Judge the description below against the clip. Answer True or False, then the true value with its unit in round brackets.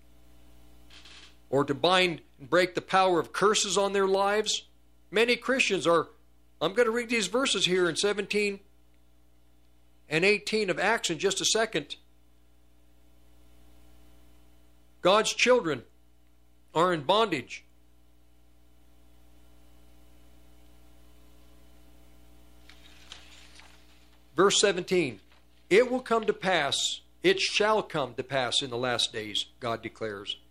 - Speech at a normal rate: False (110 wpm)